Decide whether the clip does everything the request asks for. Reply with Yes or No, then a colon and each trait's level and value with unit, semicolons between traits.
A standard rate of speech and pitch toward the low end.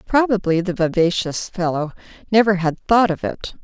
No: average, 150 wpm; high, 190 Hz